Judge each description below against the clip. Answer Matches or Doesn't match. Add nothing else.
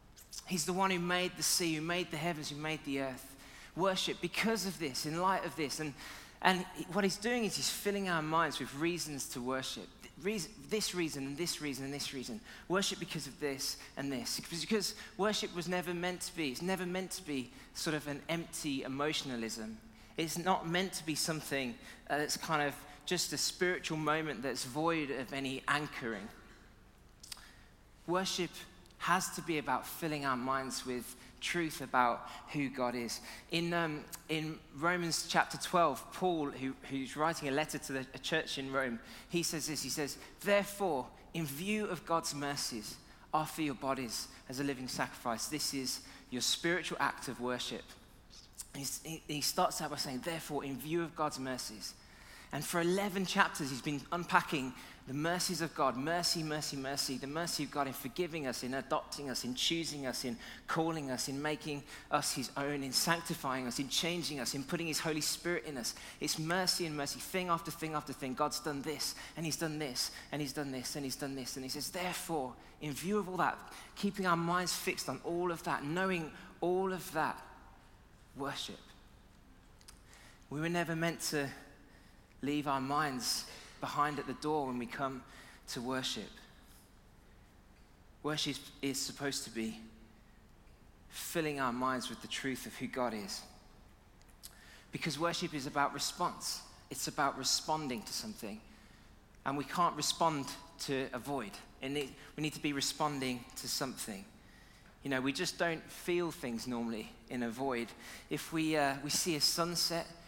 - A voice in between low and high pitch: Matches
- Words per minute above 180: Doesn't match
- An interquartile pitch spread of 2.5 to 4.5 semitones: Matches